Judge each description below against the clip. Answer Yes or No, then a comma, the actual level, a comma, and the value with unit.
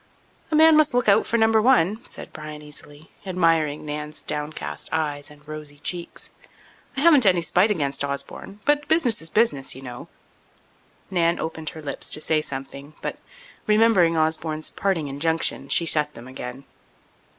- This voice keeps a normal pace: Yes, average, 160 wpm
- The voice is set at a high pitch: No, medium, 160 Hz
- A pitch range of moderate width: No, wide, 5.7 semitones